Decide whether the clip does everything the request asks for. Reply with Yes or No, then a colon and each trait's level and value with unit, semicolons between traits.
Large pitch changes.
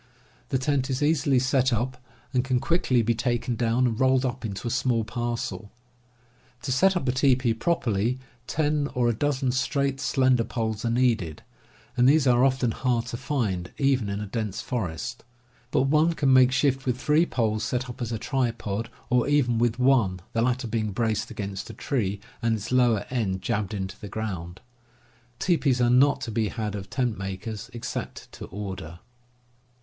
No: average, 3.2 semitones